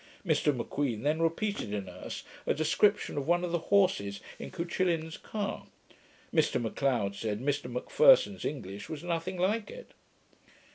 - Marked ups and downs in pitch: Yes, wide, 7.3 semitones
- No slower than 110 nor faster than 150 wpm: Yes, average, 145 wpm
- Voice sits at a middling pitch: Yes, medium, 155 Hz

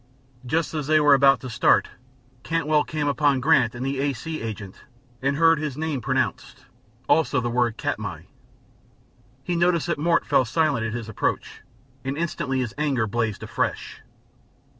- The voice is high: No, medium, 140 Hz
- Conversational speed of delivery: Yes, average, 160 wpm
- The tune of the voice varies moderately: Yes, average, 4.3 semitones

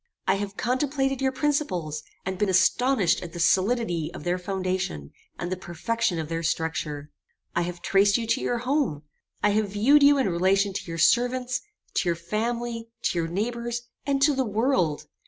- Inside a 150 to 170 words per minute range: No, average, 180 wpm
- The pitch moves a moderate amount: No, wide, 6.0 semitones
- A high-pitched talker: Yes, high, 200 Hz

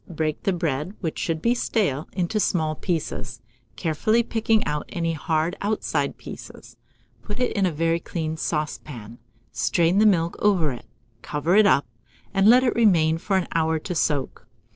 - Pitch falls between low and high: Yes, medium, 165 Hz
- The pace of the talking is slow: No, average, 165 wpm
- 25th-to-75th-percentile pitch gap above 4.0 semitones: Yes, average, 4.5 semitones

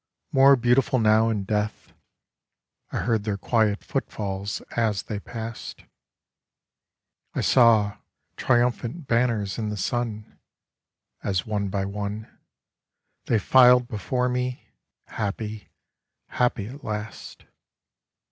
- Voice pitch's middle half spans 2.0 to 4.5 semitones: Yes, average, 2.9 semitones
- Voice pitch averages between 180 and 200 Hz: No, low, 110 Hz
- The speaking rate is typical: No, slow, 105 wpm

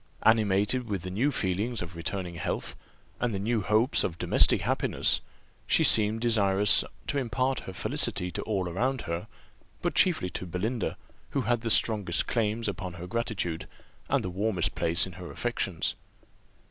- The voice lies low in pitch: Yes, low, 105 Hz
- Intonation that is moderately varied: Yes, average, 4.3 semitones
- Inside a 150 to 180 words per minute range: Yes, average, 160 wpm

